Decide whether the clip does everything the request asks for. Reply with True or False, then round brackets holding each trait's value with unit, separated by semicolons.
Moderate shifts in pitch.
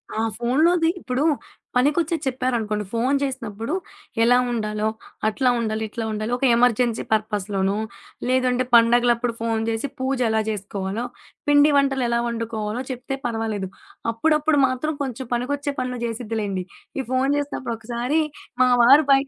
True (3.2 semitones)